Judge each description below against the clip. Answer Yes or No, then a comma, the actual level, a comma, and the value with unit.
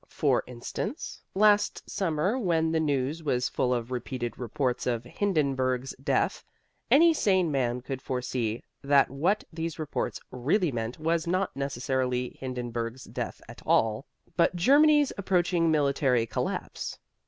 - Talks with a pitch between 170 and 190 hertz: No, medium, 140 Hz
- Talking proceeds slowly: Yes, slow, 130 wpm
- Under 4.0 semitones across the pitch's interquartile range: No, wide, 5.4 semitones